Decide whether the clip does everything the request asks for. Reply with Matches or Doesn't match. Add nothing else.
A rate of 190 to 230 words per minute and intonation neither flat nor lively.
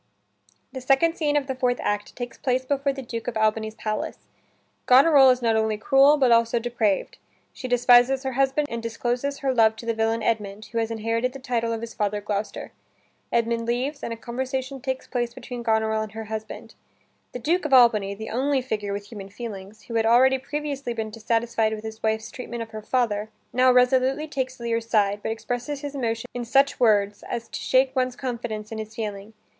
Matches